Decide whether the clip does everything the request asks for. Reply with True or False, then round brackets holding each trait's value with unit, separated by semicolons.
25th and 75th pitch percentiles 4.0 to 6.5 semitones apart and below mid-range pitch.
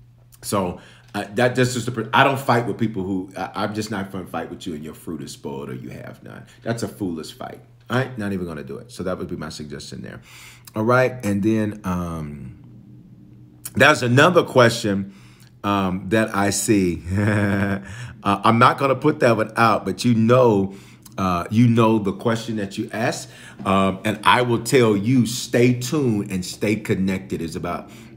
True (4.3 semitones; 105 Hz)